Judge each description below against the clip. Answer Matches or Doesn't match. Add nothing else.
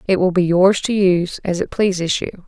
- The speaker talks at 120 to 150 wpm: Doesn't match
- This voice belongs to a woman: Matches